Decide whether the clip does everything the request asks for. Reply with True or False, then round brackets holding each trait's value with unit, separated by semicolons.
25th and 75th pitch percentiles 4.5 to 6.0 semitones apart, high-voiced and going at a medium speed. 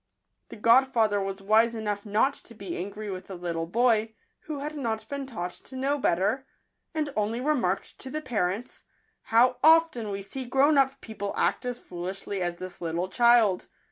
True (5.2 semitones; 220 Hz; 185 wpm)